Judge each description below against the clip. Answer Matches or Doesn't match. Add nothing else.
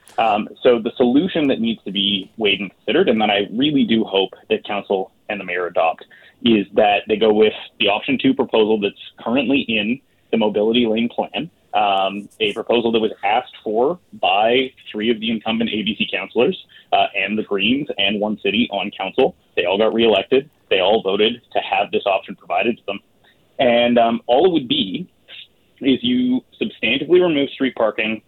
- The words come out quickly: Doesn't match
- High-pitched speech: Doesn't match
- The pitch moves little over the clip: Doesn't match